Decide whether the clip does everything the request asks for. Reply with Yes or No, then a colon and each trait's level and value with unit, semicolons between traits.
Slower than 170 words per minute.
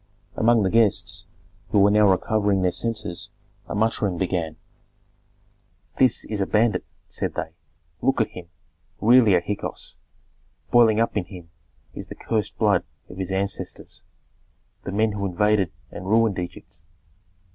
Yes: average, 145 wpm